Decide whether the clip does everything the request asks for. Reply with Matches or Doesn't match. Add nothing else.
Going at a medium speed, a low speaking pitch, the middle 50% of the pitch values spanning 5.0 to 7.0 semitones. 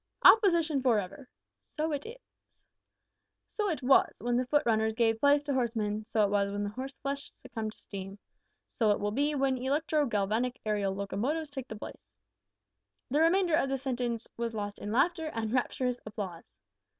Doesn't match